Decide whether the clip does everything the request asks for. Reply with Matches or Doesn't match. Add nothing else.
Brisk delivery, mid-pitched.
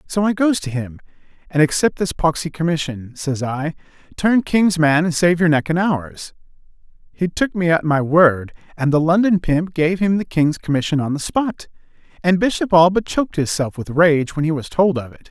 Matches